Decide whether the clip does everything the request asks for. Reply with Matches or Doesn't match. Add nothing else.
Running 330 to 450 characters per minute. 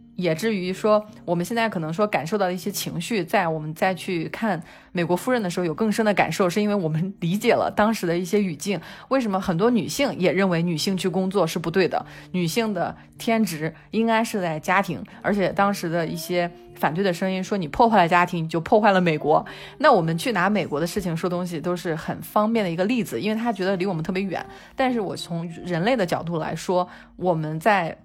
Matches